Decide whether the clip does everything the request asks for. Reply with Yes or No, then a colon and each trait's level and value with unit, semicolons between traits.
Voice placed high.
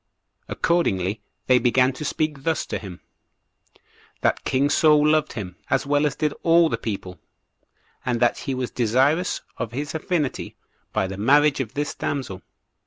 No: low, 135 Hz